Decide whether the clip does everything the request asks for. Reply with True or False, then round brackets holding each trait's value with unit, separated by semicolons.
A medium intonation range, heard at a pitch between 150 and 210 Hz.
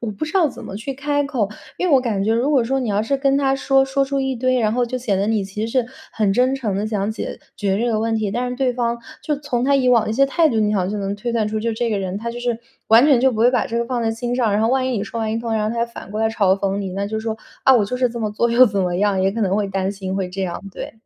False (3.5 semitones; 230 Hz)